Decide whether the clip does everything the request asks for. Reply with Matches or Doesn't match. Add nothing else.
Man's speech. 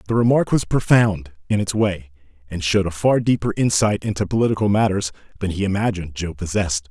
Matches